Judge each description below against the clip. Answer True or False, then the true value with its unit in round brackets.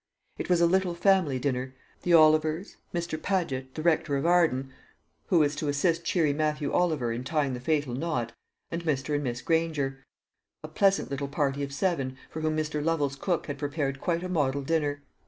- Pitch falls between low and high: True (150 Hz)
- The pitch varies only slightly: False (3.5 semitones)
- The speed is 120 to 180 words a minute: False (190 wpm)